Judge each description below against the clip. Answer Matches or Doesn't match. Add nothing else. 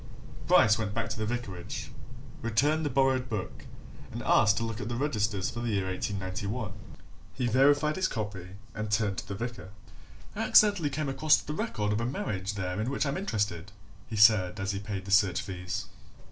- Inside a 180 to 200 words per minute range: Matches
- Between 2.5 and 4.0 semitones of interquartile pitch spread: Doesn't match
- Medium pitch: Doesn't match